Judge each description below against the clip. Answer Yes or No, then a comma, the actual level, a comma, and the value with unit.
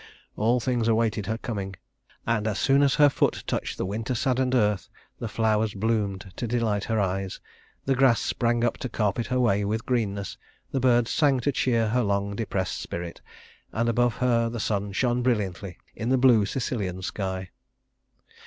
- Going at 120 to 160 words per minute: No, average, 175 wpm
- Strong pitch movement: No, average, 3.4 semitones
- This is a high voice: No, low, 115 Hz